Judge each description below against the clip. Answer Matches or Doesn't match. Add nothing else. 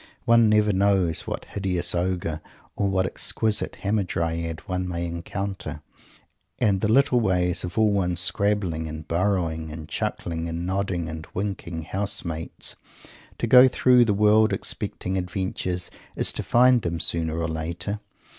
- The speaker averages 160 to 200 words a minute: Doesn't match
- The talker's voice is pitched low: Matches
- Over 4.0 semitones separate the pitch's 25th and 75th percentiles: Doesn't match